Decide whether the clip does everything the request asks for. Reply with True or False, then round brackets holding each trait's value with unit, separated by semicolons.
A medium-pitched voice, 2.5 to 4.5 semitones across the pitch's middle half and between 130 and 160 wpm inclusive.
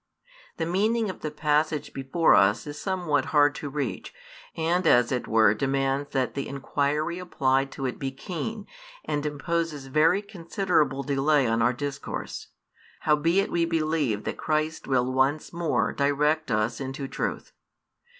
True (145 Hz; 3.5 semitones; 150 wpm)